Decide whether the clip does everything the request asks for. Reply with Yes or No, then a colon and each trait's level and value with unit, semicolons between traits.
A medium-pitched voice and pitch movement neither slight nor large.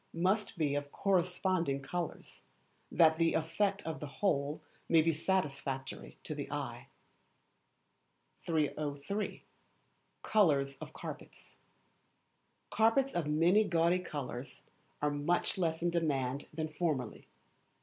Yes: medium, 160 Hz; average, 3.9 semitones